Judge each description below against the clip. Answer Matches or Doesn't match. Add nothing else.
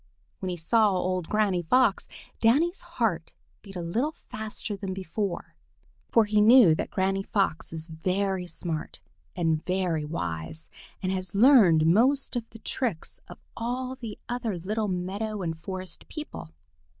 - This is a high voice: Matches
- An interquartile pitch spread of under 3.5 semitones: Doesn't match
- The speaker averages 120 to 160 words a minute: Matches